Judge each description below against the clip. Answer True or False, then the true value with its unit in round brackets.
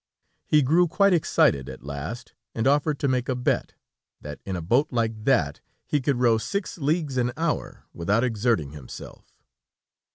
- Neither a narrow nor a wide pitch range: False (6.0 semitones)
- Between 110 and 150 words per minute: False (165 wpm)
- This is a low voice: True (125 Hz)